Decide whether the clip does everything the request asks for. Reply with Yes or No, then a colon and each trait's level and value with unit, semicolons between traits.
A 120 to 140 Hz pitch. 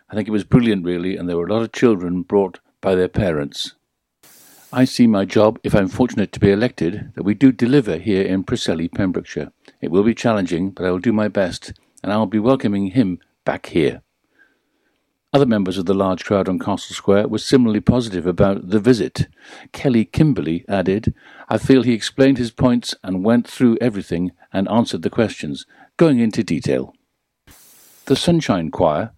No: low, 105 Hz